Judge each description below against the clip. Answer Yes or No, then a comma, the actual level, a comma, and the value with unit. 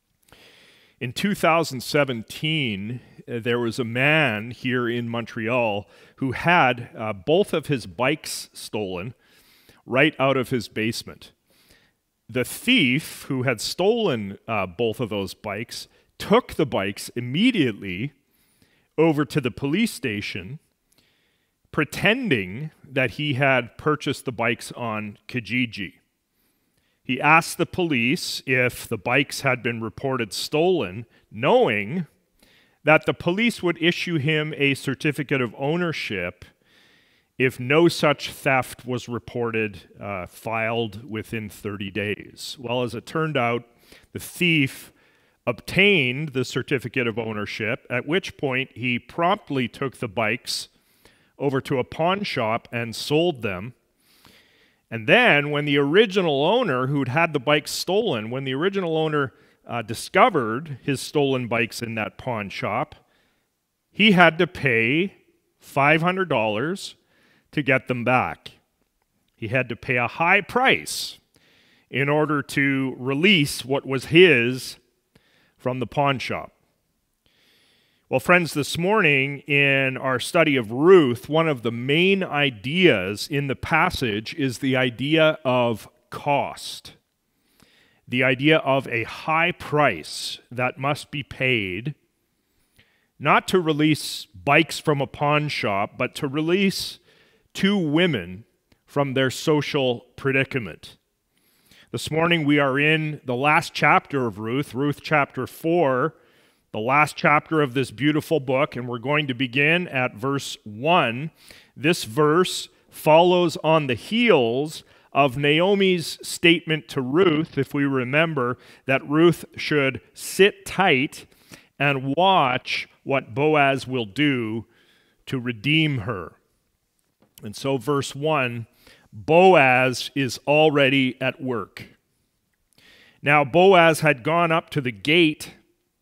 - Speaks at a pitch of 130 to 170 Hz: Yes, low, 135 Hz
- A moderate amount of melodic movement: Yes, average, 4.3 semitones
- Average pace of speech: No, slow, 125 wpm